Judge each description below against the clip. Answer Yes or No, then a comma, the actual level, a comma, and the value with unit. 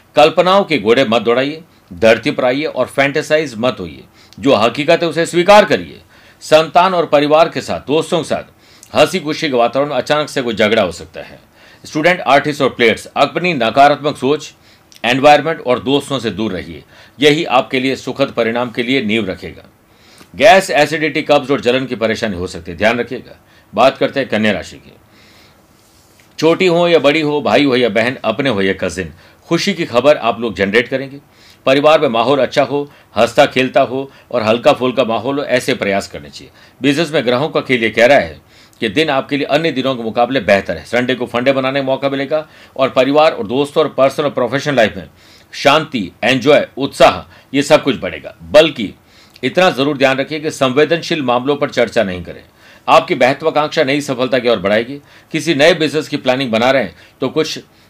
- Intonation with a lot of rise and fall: No, average, 4.6 semitones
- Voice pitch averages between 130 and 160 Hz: Yes, low, 135 Hz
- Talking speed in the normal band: No, fast, 195 wpm